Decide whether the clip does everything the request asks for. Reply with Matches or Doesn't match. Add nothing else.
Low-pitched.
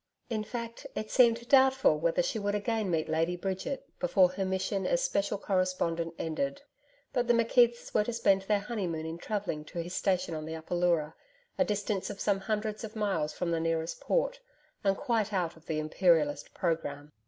Doesn't match